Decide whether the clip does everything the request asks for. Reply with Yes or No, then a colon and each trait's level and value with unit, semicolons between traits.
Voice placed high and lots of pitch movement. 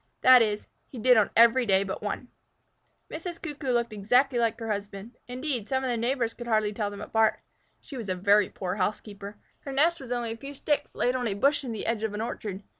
No: high, 230 Hz; average, 3.7 semitones